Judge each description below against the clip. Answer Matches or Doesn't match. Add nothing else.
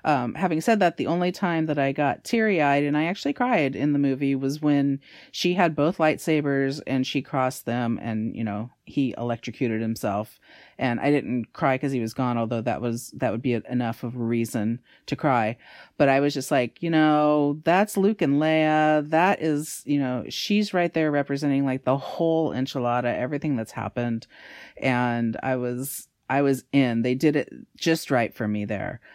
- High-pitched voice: Doesn't match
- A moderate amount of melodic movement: Matches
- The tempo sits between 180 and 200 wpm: Matches